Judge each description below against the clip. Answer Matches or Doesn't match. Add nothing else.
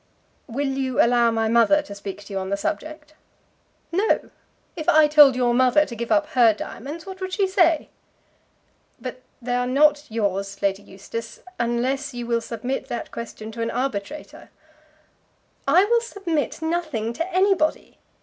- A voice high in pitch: Matches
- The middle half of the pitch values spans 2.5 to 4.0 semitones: Doesn't match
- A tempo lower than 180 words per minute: Matches